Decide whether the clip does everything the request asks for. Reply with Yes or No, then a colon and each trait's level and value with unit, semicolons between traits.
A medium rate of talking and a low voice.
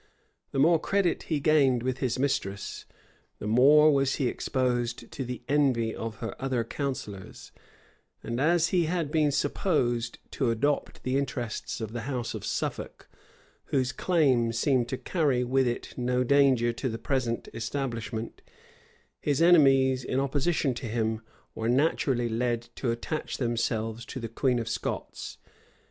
Yes: average, 150 wpm; low, 130 Hz